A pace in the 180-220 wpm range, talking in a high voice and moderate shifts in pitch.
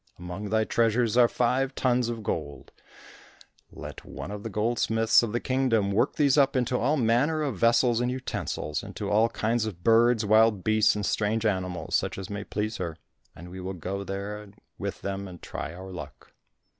No: average, 185 wpm; low, 110 Hz; average, 3.5 semitones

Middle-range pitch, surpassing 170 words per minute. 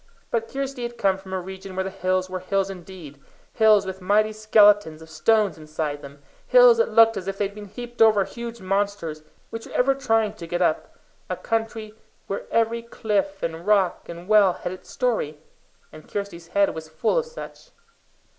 No: high, 200 Hz; average, 195 wpm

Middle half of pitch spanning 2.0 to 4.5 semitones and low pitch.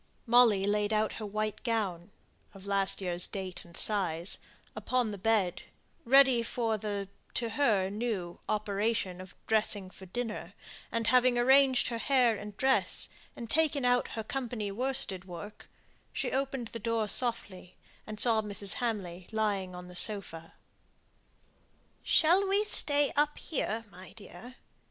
No: average, 3.9 semitones; high, 215 Hz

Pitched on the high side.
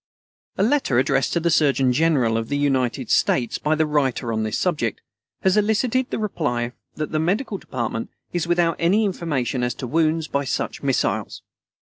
No: medium, 150 Hz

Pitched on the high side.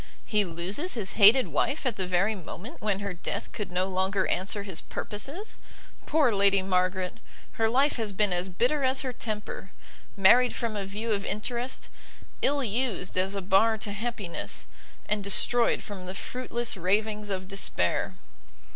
Yes: high, 205 Hz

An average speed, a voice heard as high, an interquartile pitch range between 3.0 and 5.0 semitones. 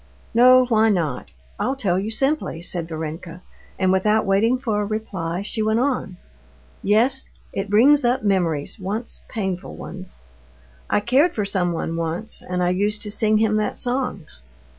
Yes: average, 160 wpm; high, 205 Hz; average, 4.0 semitones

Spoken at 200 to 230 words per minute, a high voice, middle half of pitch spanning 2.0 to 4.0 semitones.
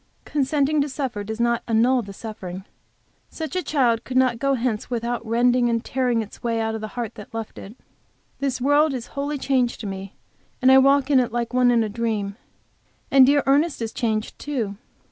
Yes: fast, 205 wpm; high, 240 Hz; average, 3.3 semitones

